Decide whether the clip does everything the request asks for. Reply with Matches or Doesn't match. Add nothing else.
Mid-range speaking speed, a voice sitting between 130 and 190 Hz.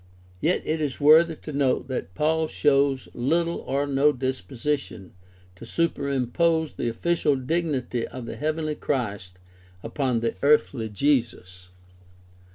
Doesn't match